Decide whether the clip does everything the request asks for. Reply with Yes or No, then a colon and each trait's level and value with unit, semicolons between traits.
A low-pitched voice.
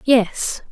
No: high, 235 Hz